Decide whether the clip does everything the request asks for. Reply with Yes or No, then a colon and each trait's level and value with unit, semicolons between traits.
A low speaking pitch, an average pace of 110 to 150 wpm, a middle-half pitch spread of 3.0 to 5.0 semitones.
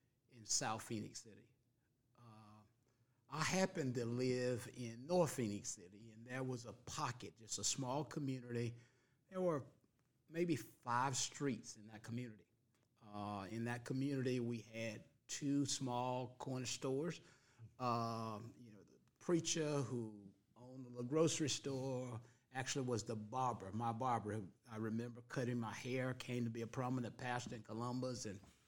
No: low, 125 Hz; average, 145 wpm; narrow, 2.6 semitones